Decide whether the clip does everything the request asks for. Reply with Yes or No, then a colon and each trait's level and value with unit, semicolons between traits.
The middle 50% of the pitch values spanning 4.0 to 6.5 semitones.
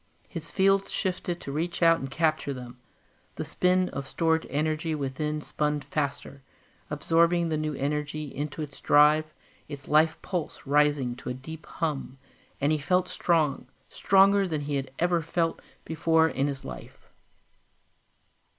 No: average, 2.7 semitones